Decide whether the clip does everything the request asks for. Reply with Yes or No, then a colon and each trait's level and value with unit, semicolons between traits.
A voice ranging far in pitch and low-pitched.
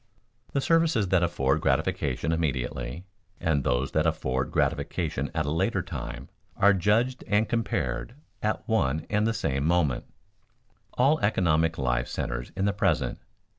Yes: wide, 7.1 semitones; very low, 85 Hz